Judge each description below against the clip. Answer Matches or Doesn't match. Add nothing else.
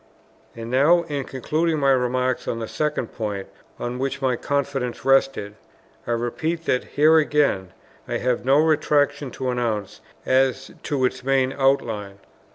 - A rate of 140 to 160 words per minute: Matches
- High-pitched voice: Doesn't match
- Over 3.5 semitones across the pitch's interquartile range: Doesn't match